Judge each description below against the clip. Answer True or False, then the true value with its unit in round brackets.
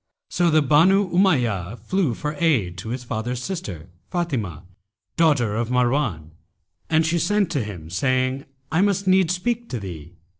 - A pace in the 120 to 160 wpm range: True (155 wpm)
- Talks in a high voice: False (135 Hz)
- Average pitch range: False (7.9 semitones)